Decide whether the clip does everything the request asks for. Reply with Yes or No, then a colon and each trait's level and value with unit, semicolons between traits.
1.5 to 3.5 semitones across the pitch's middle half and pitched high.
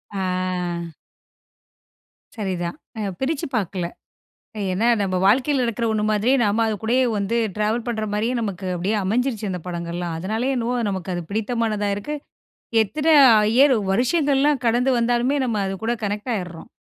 No: average, 4.0 semitones; high, 220 Hz